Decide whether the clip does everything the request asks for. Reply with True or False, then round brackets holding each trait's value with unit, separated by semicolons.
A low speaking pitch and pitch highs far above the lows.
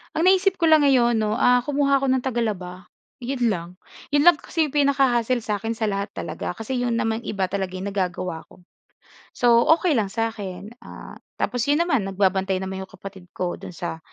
False (225 Hz; 5.7 semitones)